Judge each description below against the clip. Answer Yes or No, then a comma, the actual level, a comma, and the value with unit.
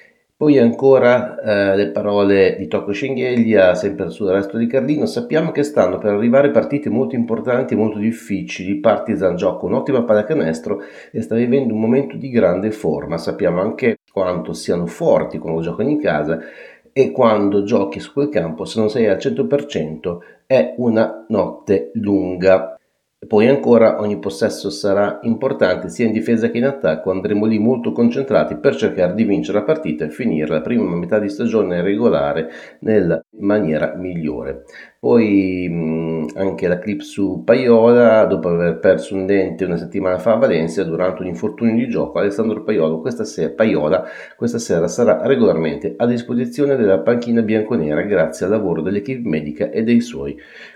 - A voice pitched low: Yes, low, 105 Hz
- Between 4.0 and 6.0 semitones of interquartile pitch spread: Yes, average, 4.3 semitones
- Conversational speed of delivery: Yes, average, 160 wpm